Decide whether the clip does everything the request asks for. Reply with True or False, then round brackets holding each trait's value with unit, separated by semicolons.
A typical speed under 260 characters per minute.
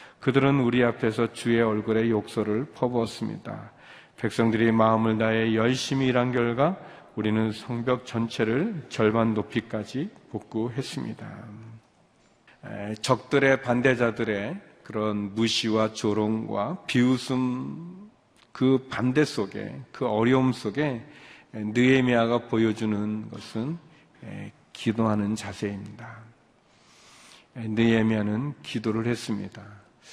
True (240 characters per minute)